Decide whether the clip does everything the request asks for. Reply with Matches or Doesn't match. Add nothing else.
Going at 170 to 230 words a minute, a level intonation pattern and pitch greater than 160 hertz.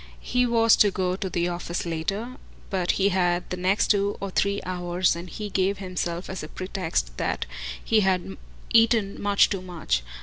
Matches